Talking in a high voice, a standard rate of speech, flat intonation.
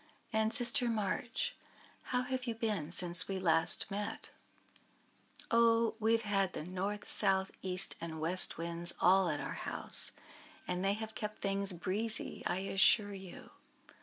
No: high, 195 Hz; average, 150 wpm; average, 3.4 semitones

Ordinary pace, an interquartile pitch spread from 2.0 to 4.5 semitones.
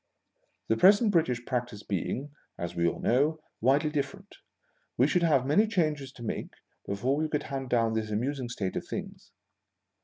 No: average, 165 wpm; average, 5.1 semitones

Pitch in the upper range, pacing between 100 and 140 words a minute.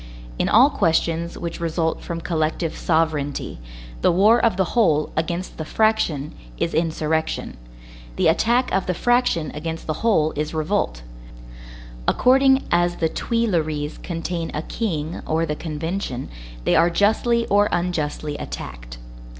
No: medium, 165 Hz; slow, 135 wpm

